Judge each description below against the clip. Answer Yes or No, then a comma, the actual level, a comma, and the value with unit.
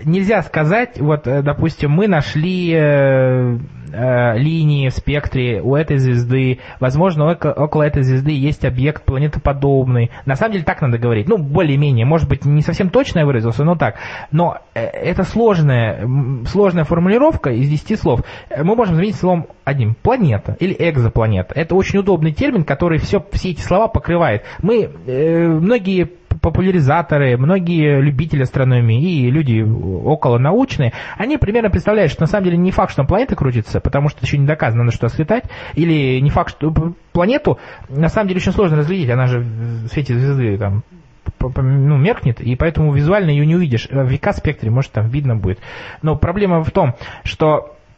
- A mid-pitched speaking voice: Yes, medium, 145 Hz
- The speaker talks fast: Yes, fast, 170 wpm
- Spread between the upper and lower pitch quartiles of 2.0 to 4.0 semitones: No, average, 5.0 semitones